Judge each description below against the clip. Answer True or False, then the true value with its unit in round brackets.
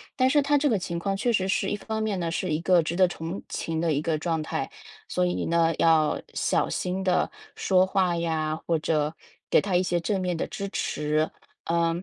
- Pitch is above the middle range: False (170 Hz)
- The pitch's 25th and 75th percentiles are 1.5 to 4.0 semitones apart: True (2.9 semitones)